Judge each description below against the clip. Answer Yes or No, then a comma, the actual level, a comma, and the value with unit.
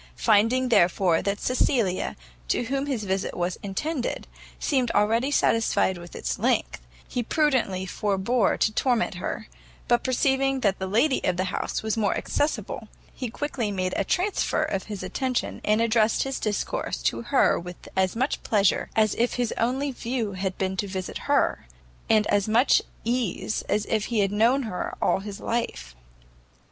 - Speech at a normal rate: Yes, average, 165 wpm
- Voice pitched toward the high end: Yes, high, 220 Hz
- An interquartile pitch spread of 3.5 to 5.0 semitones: Yes, average, 4.6 semitones